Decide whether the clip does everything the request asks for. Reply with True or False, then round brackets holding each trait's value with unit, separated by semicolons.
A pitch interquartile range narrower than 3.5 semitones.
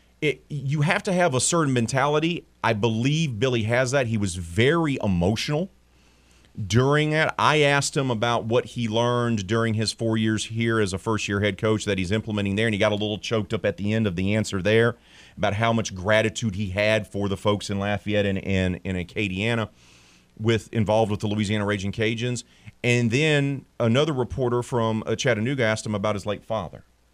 True (2.9 semitones)